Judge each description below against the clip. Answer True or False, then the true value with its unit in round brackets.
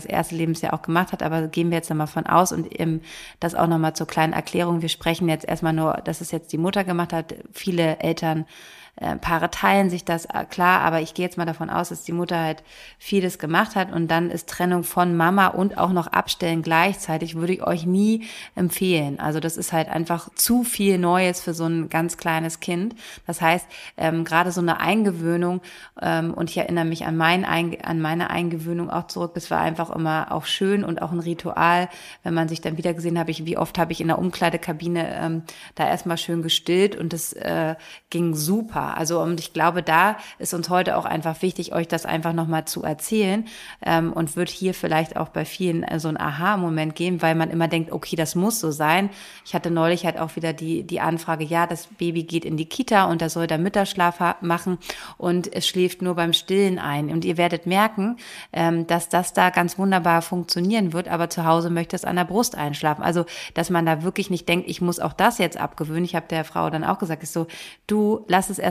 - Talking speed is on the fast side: True (220 wpm)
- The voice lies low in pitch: False (170 Hz)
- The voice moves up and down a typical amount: False (1.6 semitones)